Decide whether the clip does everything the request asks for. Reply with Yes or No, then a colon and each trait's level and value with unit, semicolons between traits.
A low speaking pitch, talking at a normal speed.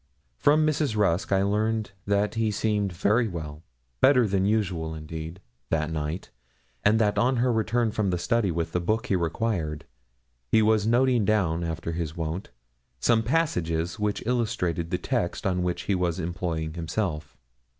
Yes: very low, 95 Hz; average, 165 wpm